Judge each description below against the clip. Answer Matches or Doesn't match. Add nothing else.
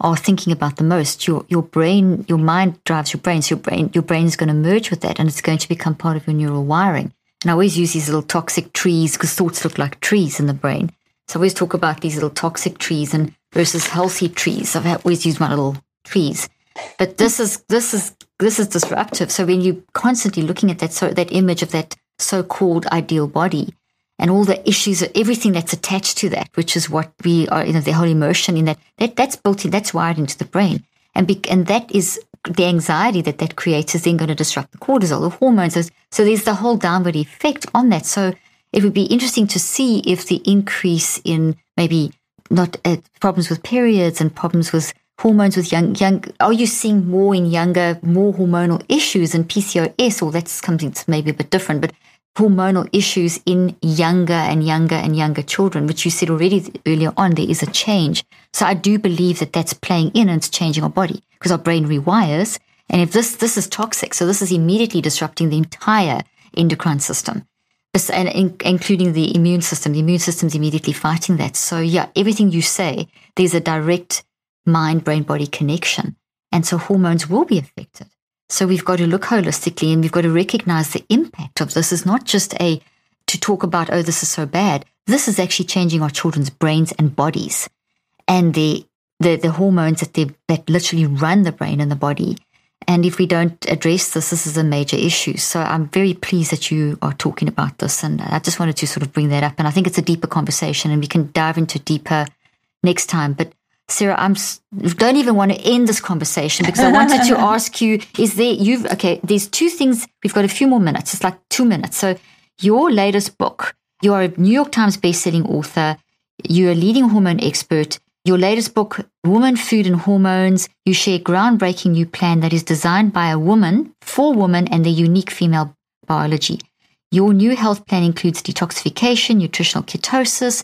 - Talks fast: Matches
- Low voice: Doesn't match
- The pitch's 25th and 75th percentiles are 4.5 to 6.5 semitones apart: Doesn't match